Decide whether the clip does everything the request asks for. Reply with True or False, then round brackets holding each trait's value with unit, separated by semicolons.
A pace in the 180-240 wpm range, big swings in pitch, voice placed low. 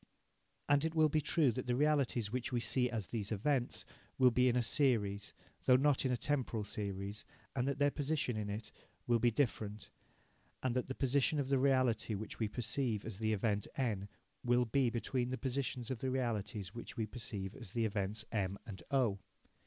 False (200 wpm; 3.7 semitones; 120 Hz)